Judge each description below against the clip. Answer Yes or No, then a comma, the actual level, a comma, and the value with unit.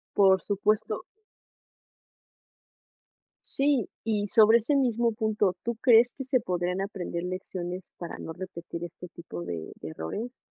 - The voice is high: Yes, high, 200 Hz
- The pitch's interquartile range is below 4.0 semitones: No, average, 4.5 semitones